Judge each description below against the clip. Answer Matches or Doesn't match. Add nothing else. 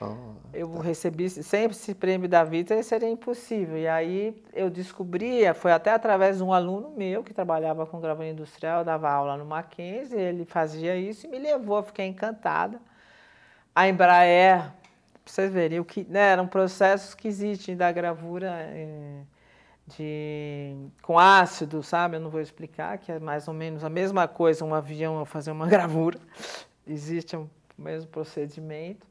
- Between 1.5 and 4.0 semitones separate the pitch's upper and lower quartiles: Matches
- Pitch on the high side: Doesn't match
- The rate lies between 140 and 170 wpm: Matches